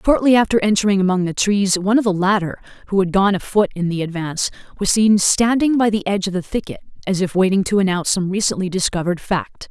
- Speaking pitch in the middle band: No, high, 195 Hz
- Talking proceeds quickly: Yes, fast, 215 wpm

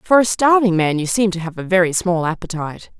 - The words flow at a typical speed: No, fast, 240 wpm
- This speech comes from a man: No, female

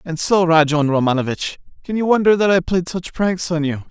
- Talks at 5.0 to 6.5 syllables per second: Yes, 5.4 syllables/s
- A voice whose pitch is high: No, medium, 170 Hz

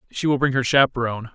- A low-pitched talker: Yes, low, 125 Hz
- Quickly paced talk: Yes, fast, 225 wpm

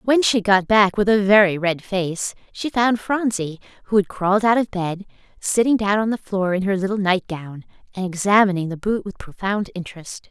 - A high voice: Yes, high, 200 Hz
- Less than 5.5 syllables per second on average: Yes, 5.0 syllables/s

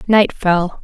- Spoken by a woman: Yes, female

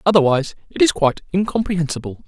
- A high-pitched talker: No, medium, 170 Hz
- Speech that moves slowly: Yes, slow, 130 wpm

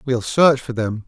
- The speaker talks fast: Yes, fast, 225 wpm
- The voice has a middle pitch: No, low, 125 Hz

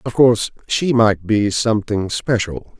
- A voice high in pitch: No, low, 110 Hz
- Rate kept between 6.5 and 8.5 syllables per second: No, 4.4 syllables/s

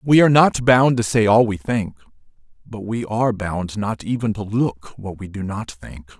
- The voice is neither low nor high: No, low, 110 Hz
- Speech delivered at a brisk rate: Yes, fast, 215 wpm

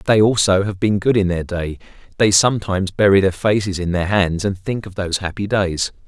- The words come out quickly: Yes, fast, 215 wpm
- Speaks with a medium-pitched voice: No, very low, 95 Hz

